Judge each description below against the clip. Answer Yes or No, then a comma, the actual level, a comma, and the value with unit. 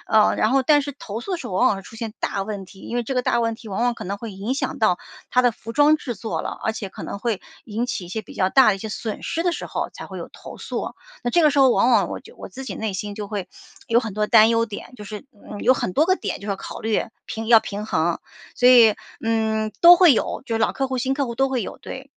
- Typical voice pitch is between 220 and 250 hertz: Yes, high, 225 Hz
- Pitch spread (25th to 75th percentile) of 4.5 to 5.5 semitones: No, average, 3.5 semitones